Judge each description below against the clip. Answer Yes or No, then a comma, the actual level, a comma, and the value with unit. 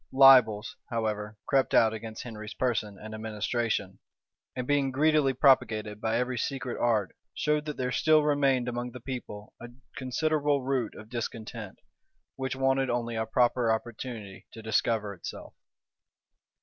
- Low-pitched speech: Yes, low, 120 Hz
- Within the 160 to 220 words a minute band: No, average, 140 wpm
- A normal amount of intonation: Yes, average, 3.4 semitones